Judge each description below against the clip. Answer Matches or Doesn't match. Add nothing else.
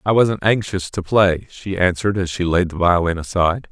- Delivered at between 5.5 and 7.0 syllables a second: Doesn't match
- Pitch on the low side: Matches